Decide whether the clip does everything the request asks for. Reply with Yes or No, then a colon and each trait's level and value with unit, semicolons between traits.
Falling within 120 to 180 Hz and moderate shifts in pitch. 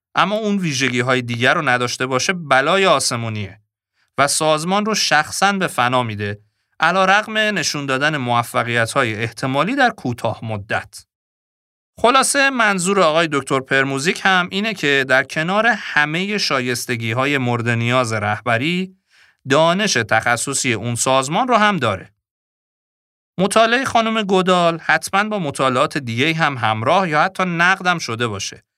No: medium, 140 Hz; wide, 8.0 semitones